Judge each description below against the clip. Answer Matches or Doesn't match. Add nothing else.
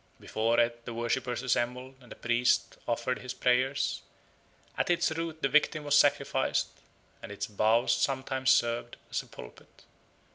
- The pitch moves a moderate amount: Doesn't match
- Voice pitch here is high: Doesn't match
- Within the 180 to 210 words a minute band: Doesn't match